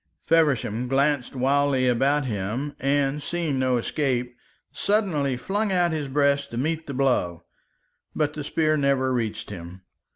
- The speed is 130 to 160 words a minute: Yes, average, 140 wpm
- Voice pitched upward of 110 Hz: Yes, medium, 140 Hz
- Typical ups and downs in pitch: Yes, average, 3.0 semitones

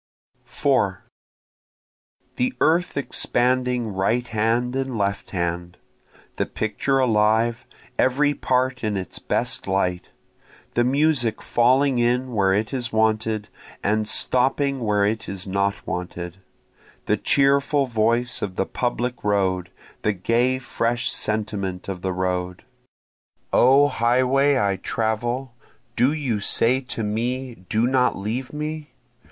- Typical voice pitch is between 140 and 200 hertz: No, low, 115 Hz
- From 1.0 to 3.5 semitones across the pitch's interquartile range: No, average, 4.1 semitones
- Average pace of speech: No, slow, 125 wpm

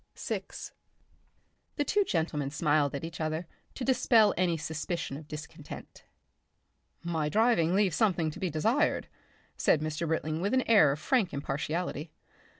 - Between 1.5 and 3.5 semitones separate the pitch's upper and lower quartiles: No, average, 4.8 semitones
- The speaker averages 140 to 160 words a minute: Yes, average, 150 wpm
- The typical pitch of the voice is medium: Yes, medium, 165 Hz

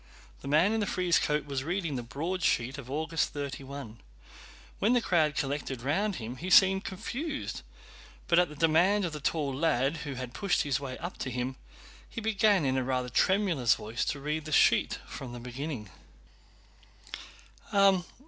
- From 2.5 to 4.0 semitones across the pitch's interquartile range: No, wide, 5.4 semitones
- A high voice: No, medium, 150 Hz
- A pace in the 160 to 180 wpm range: Yes, average, 170 wpm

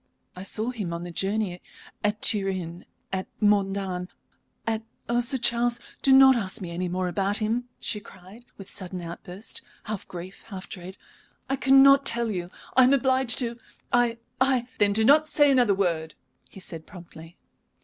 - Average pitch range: Yes, average, 4.8 semitones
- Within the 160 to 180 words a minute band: Yes, average, 175 wpm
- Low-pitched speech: No, high, 205 Hz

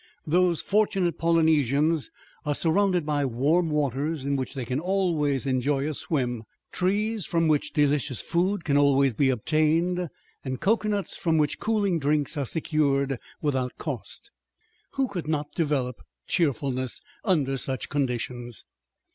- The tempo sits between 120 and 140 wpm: Yes, slow, 135 wpm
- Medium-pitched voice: Yes, medium, 150 Hz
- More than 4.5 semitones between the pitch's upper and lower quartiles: No, average, 4.0 semitones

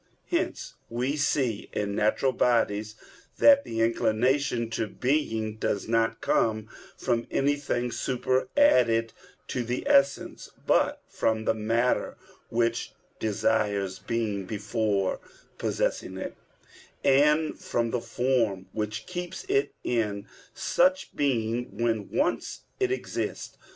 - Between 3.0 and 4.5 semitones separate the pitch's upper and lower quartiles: Yes, average, 3.6 semitones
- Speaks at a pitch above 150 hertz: No, low, 115 Hz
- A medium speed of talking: No, slow, 110 wpm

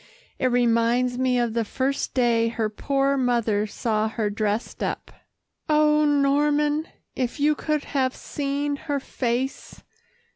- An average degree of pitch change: Yes, average, 3.6 semitones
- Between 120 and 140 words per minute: Yes, slow, 135 wpm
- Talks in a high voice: Yes, very high, 255 Hz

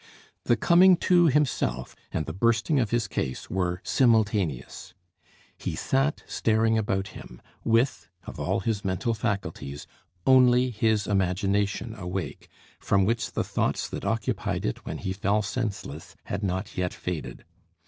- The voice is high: No, low, 105 Hz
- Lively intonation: No, average, 4.0 semitones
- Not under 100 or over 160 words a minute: Yes, average, 140 wpm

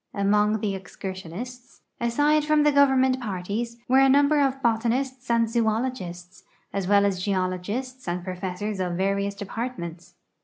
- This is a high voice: Yes, high, 215 Hz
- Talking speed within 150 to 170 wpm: No, average, 140 wpm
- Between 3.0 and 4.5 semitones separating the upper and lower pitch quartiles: No, average, 5.3 semitones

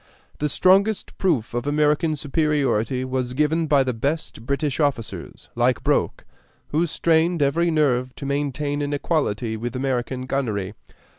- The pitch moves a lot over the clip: No, average, 3.3 semitones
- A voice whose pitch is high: No, medium, 140 Hz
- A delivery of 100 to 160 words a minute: Yes, average, 140 wpm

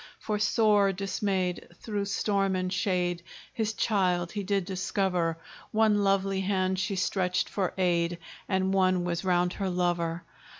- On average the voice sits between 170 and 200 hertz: Yes, high, 190 Hz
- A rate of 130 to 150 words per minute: Yes, average, 140 wpm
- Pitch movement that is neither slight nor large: No, narrow, 1.9 semitones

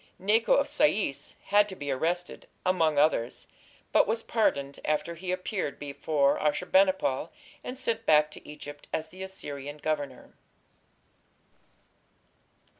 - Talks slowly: Yes, slow, 130 wpm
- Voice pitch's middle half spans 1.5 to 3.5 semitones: No, average, 4.9 semitones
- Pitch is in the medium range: Yes, medium, 160 Hz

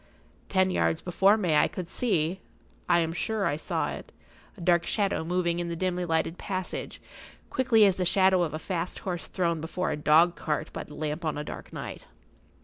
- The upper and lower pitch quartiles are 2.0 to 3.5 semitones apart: Yes, narrow, 2.5 semitones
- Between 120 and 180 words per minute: No, average, 190 wpm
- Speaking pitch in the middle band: Yes, medium, 175 Hz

